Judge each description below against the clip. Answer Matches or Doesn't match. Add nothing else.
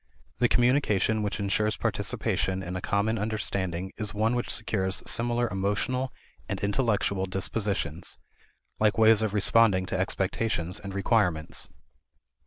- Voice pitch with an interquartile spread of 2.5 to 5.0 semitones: Matches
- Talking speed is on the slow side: Matches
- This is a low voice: Matches